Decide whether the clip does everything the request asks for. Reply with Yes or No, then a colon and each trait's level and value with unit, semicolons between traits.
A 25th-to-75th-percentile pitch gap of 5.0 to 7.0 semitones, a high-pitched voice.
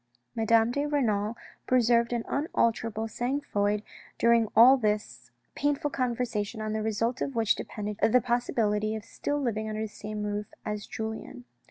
No: narrow, 2.5 semitones; high, 225 Hz